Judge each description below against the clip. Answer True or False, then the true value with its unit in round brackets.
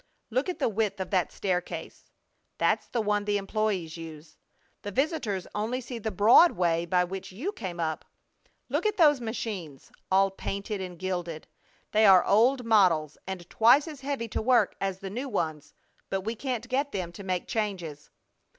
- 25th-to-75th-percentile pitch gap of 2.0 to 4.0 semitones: False (4.7 semitones)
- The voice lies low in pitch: False (200 Hz)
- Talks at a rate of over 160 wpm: True (180 wpm)